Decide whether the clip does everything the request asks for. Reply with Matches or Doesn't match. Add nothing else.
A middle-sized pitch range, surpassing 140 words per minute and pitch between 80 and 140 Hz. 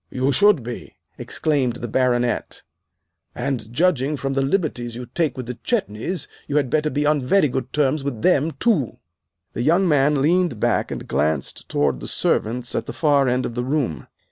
Matches